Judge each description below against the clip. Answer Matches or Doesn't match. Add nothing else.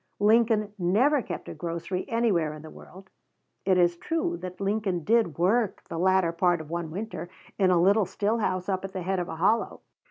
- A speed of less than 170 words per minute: Doesn't match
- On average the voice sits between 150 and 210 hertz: Matches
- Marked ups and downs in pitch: Doesn't match